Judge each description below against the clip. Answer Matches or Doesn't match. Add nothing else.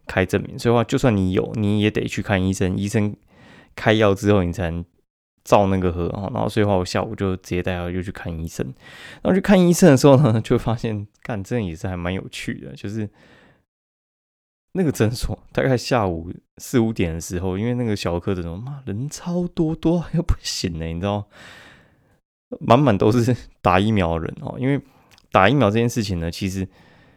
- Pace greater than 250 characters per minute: Matches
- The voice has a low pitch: Matches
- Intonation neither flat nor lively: Matches